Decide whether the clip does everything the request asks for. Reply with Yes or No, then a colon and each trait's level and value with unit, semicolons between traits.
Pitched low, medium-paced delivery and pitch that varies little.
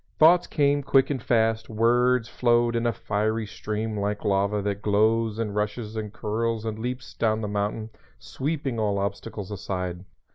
Yes: low, 110 Hz; average, 160 wpm; narrow, 2.3 semitones